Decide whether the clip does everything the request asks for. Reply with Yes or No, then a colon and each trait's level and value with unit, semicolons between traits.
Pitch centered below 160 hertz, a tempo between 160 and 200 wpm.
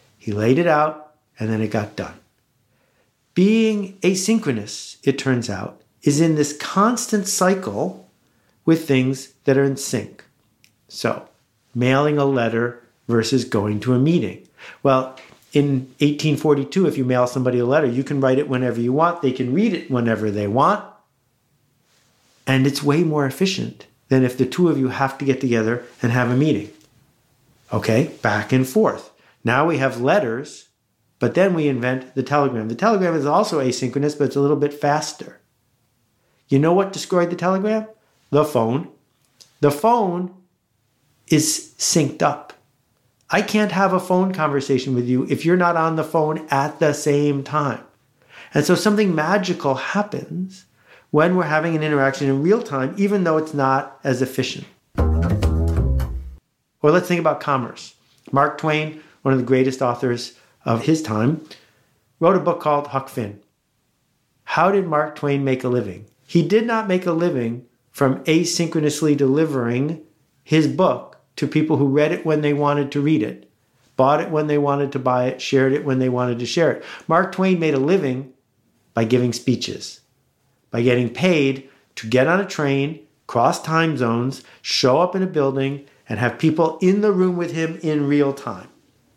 Yes: medium, 140 Hz; average, 170 wpm